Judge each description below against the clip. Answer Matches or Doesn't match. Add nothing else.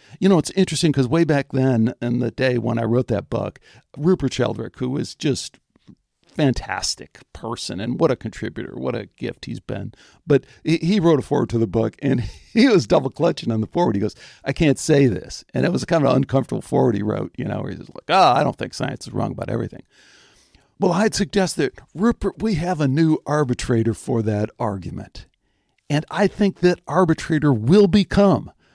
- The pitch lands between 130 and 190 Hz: Matches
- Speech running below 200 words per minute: Doesn't match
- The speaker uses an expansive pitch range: Matches